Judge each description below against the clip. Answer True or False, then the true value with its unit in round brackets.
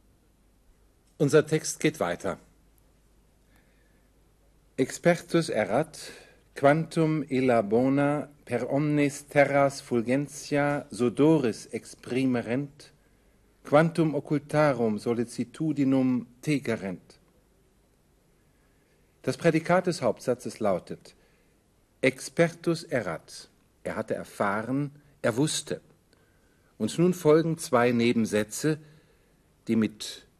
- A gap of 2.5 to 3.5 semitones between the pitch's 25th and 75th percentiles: False (4.1 semitones)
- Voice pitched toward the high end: False (140 Hz)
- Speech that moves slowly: True (75 wpm)